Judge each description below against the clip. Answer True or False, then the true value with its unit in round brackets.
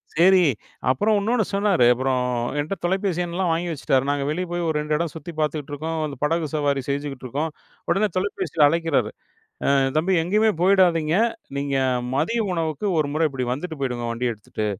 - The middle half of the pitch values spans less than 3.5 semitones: False (4.1 semitones)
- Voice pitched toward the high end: False (160 Hz)